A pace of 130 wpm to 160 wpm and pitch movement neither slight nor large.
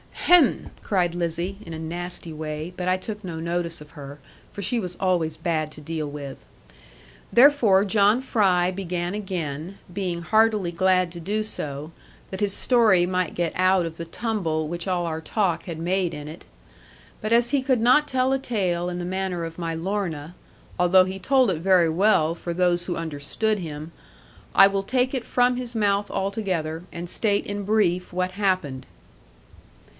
No: average, 180 wpm; average, 3.6 semitones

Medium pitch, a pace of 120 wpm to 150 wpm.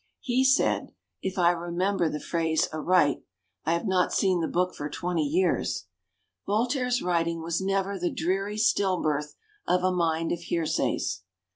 No: medium, 175 Hz; average, 160 wpm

